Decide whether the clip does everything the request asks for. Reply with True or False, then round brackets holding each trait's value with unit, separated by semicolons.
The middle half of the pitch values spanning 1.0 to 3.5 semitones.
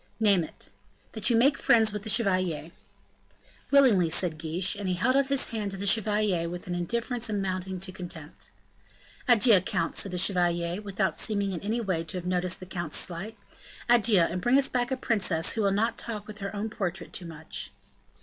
False (3.9 semitones)